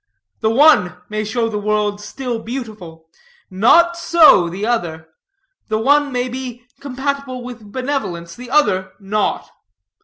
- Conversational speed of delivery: No, slow, 130 wpm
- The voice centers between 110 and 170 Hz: No, high, 230 Hz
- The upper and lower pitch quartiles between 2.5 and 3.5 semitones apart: No, average, 4.5 semitones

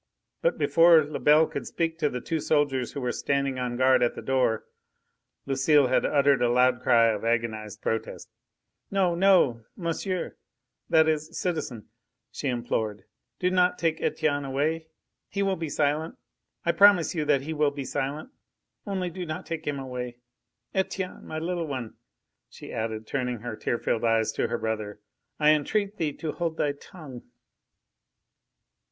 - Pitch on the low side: No, medium, 145 Hz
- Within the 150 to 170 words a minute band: Yes, average, 160 wpm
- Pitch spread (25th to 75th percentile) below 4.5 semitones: No, average, 5.0 semitones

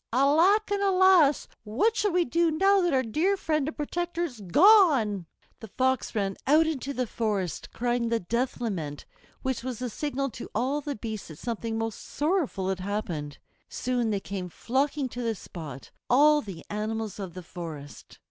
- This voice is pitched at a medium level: No, high, 245 Hz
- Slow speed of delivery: No, average, 175 wpm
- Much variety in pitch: Yes, wide, 6.9 semitones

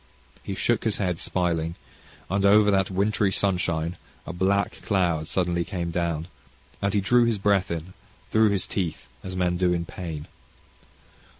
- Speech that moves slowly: No, average, 160 wpm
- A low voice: Yes, very low, 95 Hz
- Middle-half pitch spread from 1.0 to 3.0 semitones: Yes, narrow, 2.6 semitones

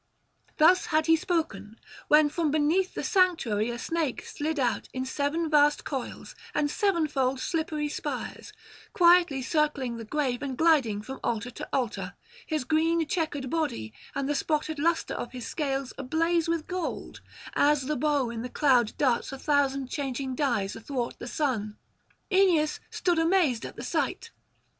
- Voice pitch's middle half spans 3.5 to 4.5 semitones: Yes, average, 4.0 semitones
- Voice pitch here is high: Yes, very high, 290 Hz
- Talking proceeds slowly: No, average, 155 wpm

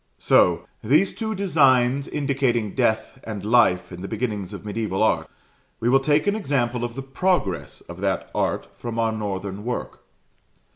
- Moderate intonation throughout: Yes, average, 4.5 semitones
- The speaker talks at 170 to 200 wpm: No, average, 160 wpm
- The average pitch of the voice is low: Yes, low, 120 Hz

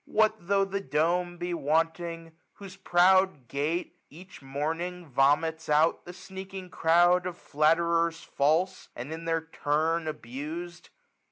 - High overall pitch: No, medium, 165 Hz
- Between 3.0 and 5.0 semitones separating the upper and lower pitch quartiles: No, narrow, 2.4 semitones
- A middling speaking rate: No, slow, 125 wpm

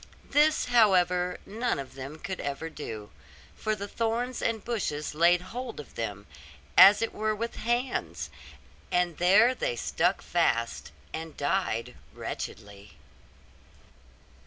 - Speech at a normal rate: No, slow, 125 wpm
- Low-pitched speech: No, medium, 180 Hz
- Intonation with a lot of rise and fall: Yes, wide, 8.4 semitones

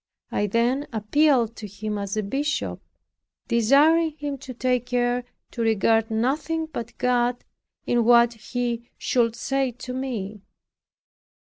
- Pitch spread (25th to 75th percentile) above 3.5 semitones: No, average, 3.1 semitones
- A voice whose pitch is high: Yes, high, 245 Hz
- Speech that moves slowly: Yes, slow, 130 wpm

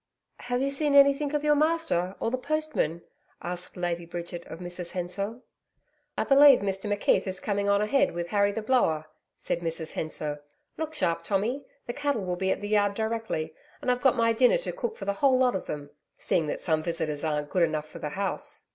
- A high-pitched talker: Yes, high, 200 Hz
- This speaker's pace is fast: Yes, fast, 210 wpm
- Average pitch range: No, wide, 7.2 semitones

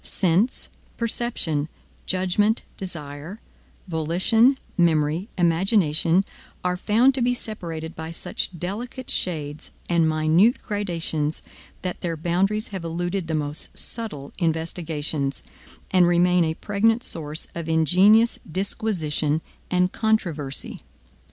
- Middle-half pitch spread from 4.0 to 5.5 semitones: Yes, average, 4.4 semitones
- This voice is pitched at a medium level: Yes, medium, 175 Hz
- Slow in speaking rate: Yes, slow, 105 wpm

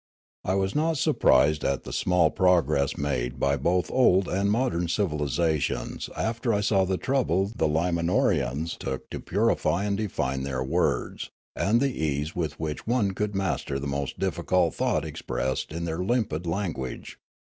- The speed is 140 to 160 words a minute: Yes, average, 155 wpm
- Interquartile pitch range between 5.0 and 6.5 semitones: Yes, wide, 5.6 semitones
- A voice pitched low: Yes, very low, 85 Hz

